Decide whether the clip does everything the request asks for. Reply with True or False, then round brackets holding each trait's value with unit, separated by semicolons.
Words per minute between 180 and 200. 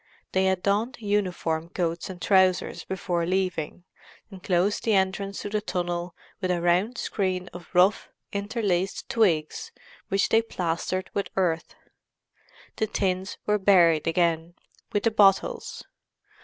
False (135 wpm)